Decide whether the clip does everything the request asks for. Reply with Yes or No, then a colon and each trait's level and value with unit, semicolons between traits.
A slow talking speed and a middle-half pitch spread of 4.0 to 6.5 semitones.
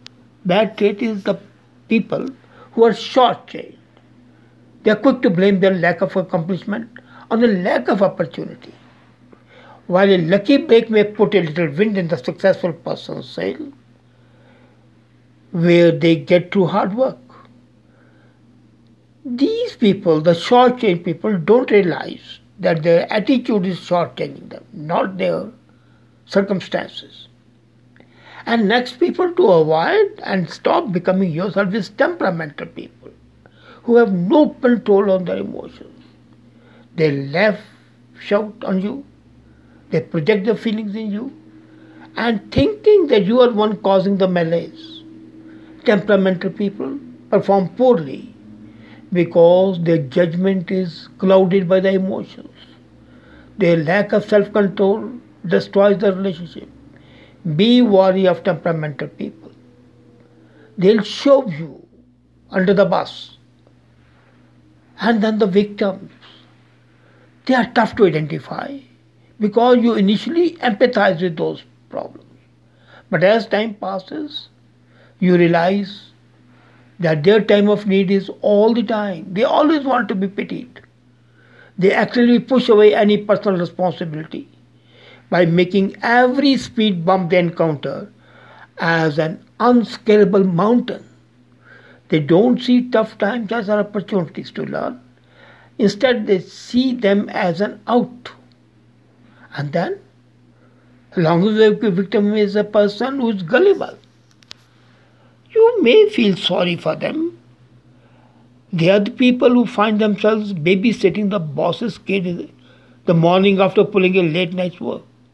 Yes: slow, 125 wpm; average, 4.5 semitones